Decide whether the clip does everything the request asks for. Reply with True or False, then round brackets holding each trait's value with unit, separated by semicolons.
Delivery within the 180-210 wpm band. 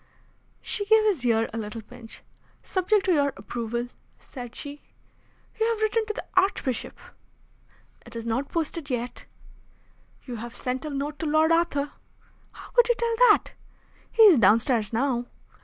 False (155 wpm)